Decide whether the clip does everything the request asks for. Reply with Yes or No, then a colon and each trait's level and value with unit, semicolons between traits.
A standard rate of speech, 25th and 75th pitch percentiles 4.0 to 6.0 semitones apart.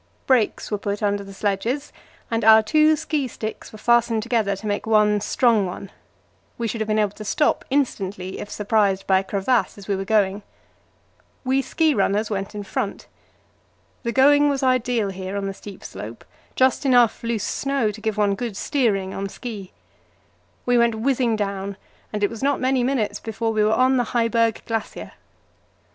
No: average, 185 wpm; average, 3.5 semitones